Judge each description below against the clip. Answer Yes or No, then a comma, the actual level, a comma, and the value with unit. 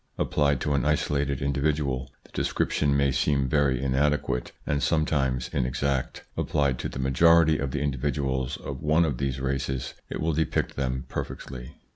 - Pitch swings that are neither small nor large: No, narrow, 2.0 semitones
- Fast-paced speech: No, average, 155 wpm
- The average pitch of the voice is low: Yes, very low, 70 Hz